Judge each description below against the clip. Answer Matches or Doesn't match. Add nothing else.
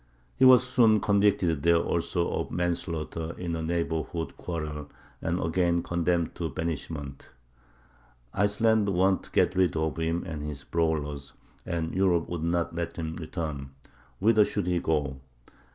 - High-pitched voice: Doesn't match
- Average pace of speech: Matches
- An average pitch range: Doesn't match